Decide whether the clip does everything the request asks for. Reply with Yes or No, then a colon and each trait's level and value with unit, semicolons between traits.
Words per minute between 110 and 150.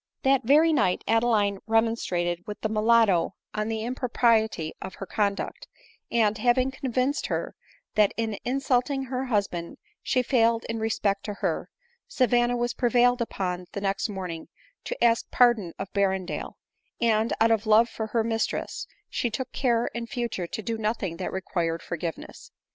No: average, 160 wpm